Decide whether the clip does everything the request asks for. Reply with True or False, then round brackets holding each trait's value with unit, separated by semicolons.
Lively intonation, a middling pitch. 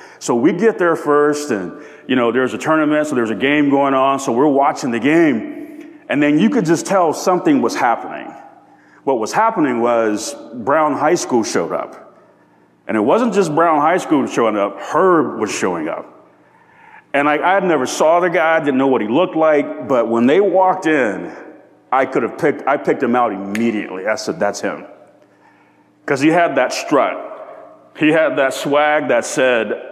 True (6.8 semitones; 155 Hz)